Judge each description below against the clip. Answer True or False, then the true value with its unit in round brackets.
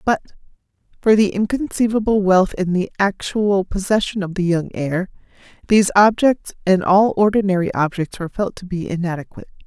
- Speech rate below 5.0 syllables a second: False (5.5 syllables/s)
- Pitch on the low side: False (195 Hz)